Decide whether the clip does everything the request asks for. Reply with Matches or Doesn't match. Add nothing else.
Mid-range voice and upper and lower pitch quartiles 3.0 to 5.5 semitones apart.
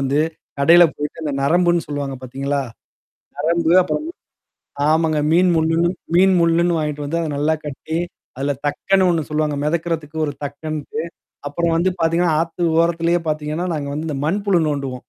Doesn't match